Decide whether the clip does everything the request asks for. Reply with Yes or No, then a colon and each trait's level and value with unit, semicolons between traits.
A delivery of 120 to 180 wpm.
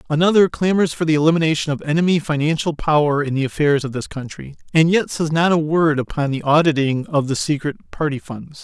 No: average, 200 wpm